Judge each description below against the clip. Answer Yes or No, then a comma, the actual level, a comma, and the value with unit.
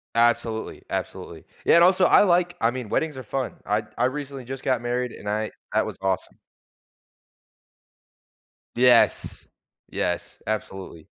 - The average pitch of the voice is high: No, low, 120 Hz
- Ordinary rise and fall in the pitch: Yes, average, 4.0 semitones